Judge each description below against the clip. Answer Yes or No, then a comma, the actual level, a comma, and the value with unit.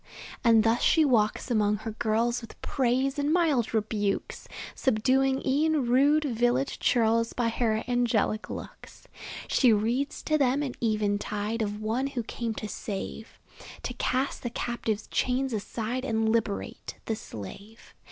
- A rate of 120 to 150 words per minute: Yes, average, 140 wpm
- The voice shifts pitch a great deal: No, average, 3.4 semitones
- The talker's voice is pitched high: Yes, high, 235 Hz